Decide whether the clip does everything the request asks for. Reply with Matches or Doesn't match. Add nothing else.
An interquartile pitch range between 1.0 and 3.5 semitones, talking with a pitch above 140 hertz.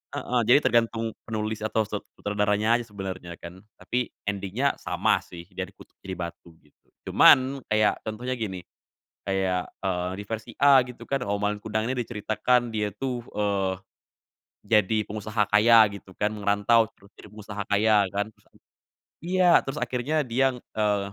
Doesn't match